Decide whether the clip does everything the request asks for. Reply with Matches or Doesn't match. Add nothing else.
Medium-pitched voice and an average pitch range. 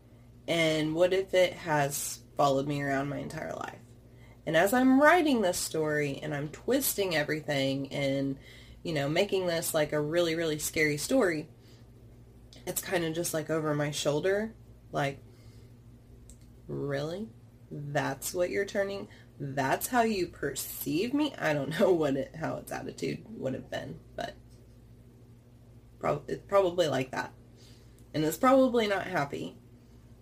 Doesn't match